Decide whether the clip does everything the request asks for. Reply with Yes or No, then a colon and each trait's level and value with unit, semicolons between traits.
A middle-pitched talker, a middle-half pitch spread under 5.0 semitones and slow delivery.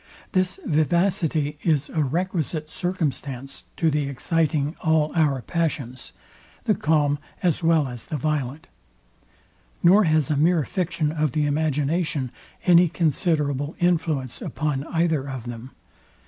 Yes: medium, 155 Hz; average, 2.8 semitones; slow, 125 wpm